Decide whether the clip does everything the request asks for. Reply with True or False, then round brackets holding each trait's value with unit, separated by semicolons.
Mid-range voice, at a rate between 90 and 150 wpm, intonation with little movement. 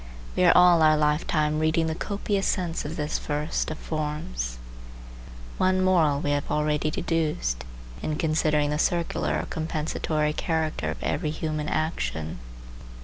True (155 Hz; 145 wpm; 1.6 semitones)